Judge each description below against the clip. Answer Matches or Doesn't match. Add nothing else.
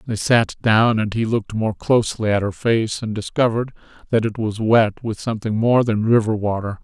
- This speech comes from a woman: Doesn't match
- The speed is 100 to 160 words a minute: Doesn't match